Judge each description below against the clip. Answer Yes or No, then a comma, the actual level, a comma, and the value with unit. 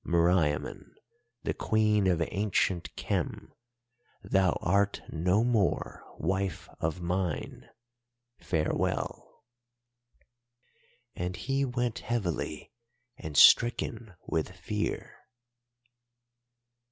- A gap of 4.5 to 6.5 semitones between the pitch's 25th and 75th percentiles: No, average, 3.8 semitones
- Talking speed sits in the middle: No, slow, 80 wpm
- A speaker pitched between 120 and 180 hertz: No, very low, 95 Hz